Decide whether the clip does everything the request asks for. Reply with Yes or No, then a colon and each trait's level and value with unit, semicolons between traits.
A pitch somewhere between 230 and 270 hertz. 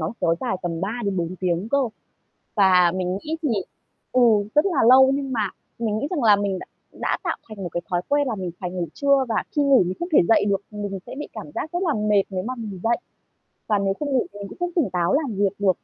No: high, 210 Hz